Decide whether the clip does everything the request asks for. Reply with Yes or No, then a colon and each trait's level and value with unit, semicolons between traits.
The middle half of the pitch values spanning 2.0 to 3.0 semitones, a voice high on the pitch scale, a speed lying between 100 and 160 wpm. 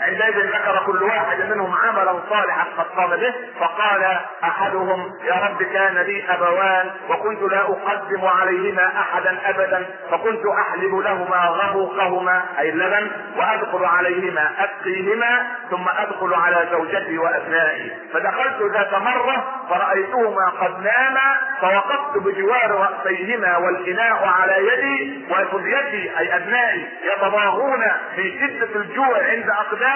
Yes: average, 2.7 semitones; high, 195 Hz; average, 115 wpm